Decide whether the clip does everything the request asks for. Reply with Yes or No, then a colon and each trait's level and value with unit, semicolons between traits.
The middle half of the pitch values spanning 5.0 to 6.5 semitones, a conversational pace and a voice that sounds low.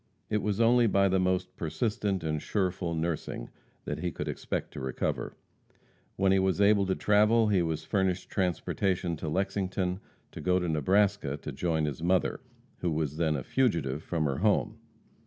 No: average, 3.8 semitones; average, 175 wpm; very low, 90 Hz